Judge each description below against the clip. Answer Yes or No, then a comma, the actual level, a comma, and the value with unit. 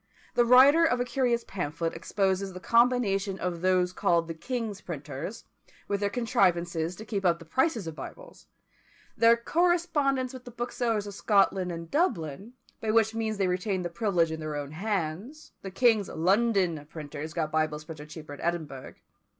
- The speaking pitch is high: Yes, high, 195 Hz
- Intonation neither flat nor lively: No, wide, 5.9 semitones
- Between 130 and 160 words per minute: No, average, 170 wpm